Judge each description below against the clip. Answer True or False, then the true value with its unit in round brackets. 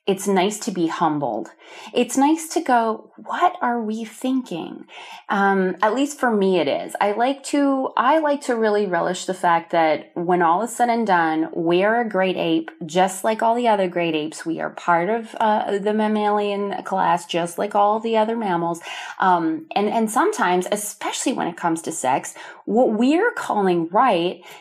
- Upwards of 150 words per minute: True (190 wpm)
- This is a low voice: False (205 Hz)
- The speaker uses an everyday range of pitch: True (4.7 semitones)